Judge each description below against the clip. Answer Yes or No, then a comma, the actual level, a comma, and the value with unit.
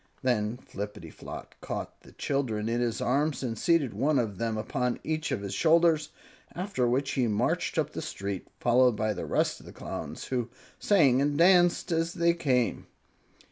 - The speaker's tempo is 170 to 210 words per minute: Yes, average, 175 wpm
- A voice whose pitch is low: Yes, low, 130 Hz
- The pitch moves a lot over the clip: Yes, wide, 5.7 semitones